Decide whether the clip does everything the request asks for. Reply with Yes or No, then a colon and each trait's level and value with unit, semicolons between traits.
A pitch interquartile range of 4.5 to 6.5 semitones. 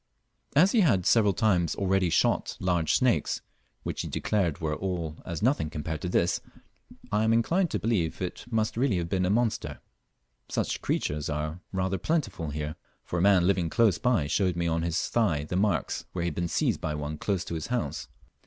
Yes: average, 4.9 semitones